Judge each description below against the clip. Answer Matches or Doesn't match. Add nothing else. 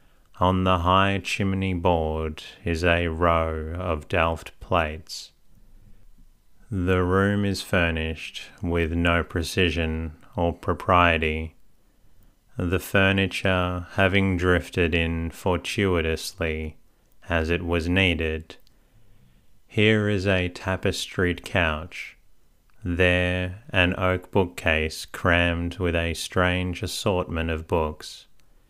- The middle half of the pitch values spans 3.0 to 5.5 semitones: Doesn't match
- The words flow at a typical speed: Doesn't match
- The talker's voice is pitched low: Matches